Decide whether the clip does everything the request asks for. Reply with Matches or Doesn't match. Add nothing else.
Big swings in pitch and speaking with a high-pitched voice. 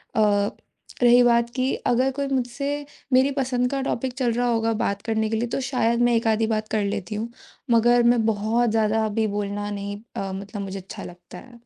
Doesn't match